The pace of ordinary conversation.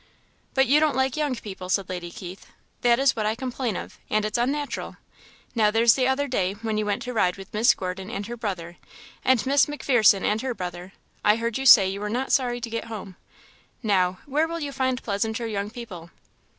No: fast, 215 wpm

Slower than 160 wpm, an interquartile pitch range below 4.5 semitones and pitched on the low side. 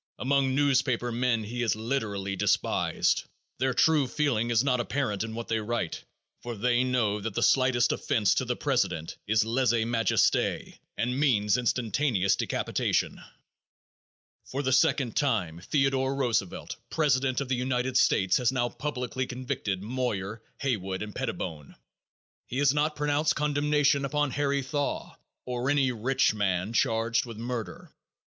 Yes: average, 145 wpm; average, 3.5 semitones; low, 125 Hz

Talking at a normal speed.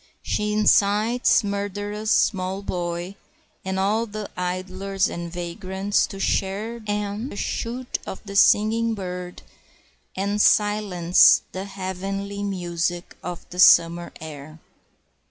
No: slow, 110 wpm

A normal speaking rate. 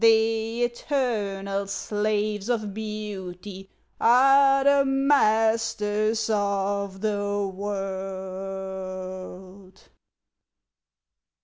No: slow, 60 wpm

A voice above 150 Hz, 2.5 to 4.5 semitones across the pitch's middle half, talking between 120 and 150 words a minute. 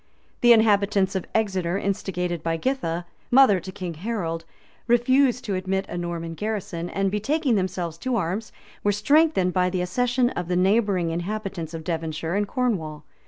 No: high, 190 Hz; average, 4.2 semitones; average, 160 wpm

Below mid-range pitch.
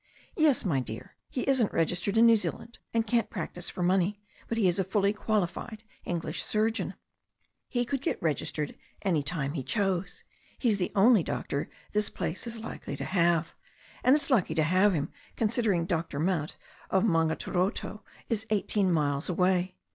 No: high, 190 Hz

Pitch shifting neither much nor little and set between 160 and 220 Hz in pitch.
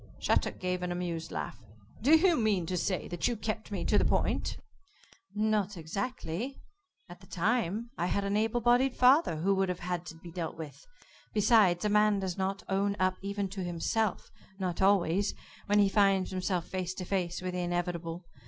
Yes: average, 3.0 semitones; high, 190 Hz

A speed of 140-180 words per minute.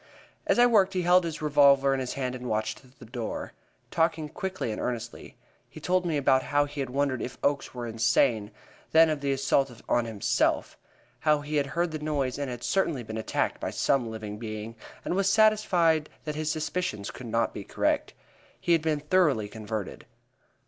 No: average, 190 wpm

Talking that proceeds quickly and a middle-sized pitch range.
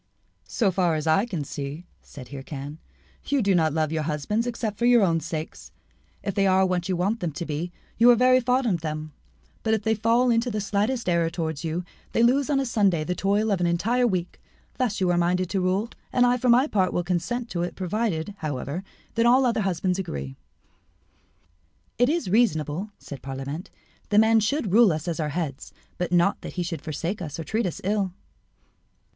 No: fast, 210 wpm; wide, 5.8 semitones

